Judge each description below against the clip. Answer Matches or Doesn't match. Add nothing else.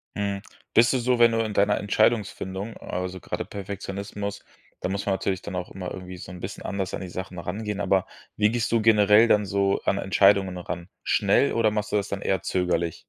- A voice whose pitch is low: Matches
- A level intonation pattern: Matches